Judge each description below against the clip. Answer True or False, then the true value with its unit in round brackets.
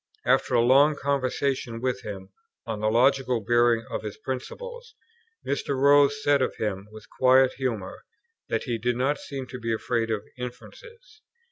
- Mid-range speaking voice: False (125 Hz)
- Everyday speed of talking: True (160 wpm)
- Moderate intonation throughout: True (3.5 semitones)